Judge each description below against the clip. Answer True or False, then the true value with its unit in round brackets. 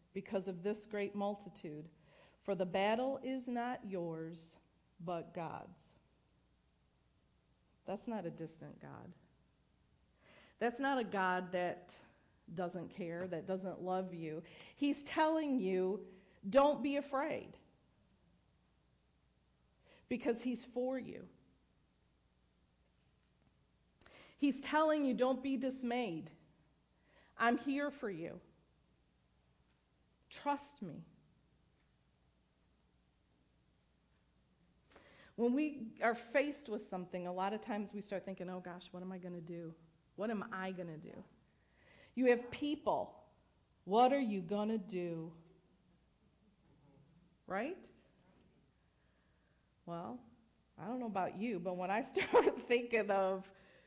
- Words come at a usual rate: False (110 wpm)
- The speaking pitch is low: False (190 Hz)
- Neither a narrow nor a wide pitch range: False (6.5 semitones)